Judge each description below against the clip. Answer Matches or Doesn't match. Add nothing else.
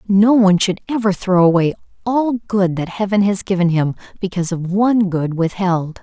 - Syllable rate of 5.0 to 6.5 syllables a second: Matches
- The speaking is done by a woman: Matches